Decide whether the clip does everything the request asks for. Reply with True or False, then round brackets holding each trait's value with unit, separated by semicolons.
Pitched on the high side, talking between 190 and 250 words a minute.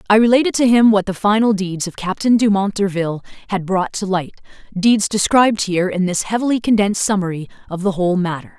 True (200 Hz; 195 wpm)